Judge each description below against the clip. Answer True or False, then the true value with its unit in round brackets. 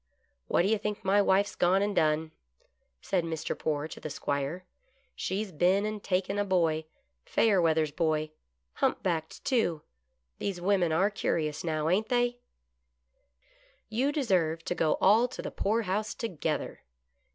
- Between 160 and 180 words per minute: True (165 wpm)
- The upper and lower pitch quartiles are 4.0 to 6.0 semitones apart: True (4.7 semitones)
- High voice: False (180 Hz)